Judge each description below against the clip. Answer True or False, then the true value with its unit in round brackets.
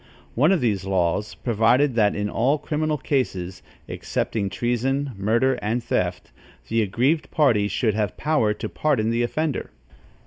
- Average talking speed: True (145 wpm)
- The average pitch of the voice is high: False (120 Hz)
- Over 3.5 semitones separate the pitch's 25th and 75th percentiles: True (5.1 semitones)